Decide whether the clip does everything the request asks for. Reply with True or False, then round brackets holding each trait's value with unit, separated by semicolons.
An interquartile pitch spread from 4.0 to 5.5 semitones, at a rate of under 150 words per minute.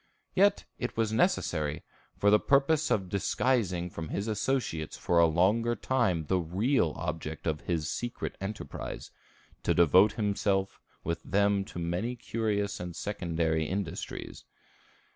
True (4.7 semitones; 135 wpm)